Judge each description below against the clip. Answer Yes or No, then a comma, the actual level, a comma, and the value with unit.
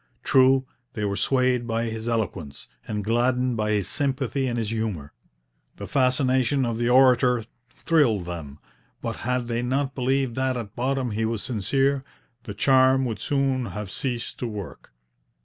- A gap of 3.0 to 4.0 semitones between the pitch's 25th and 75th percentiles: Yes, average, 3.3 semitones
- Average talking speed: Yes, average, 160 wpm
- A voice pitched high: No, low, 120 Hz